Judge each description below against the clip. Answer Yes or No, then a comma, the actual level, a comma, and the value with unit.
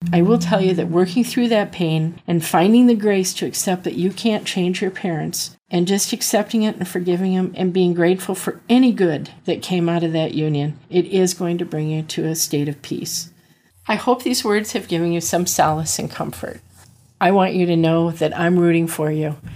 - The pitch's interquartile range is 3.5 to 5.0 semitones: No, average, 2.9 semitones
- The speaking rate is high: Yes, fast, 220 wpm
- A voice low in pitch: No, medium, 180 Hz